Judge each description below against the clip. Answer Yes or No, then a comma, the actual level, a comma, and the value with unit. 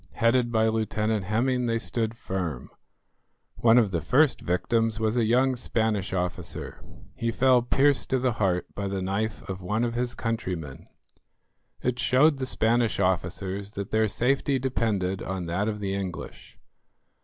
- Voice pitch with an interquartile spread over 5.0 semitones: No, average, 4.0 semitones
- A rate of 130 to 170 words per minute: Yes, average, 155 wpm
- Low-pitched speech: Yes, low, 110 Hz